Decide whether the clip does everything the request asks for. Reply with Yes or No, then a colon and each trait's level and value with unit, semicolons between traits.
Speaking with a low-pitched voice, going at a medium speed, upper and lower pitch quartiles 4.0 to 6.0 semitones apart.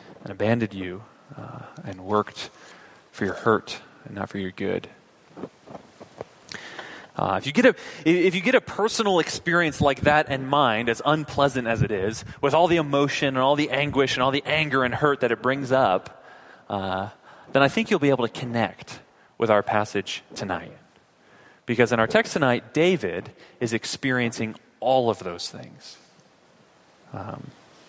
Yes: low, 130 Hz; average, 170 wpm; average, 4.8 semitones